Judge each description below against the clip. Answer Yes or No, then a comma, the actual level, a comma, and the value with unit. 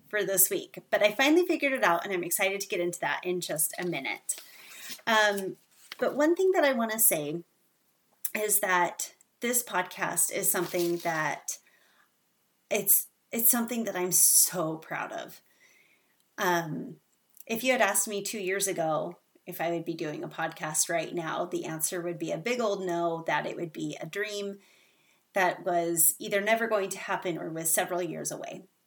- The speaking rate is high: No, average, 185 wpm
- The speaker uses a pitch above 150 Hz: Yes, medium, 185 Hz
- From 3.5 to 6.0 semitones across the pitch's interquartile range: Yes, average, 3.8 semitones